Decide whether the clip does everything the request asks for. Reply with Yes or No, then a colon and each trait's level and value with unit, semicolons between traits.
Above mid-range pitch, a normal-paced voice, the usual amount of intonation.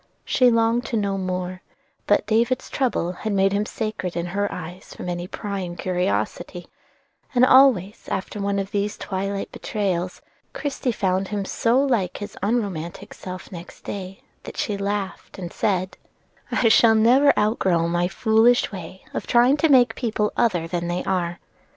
Yes: high, 200 Hz; average, 155 wpm; average, 3.8 semitones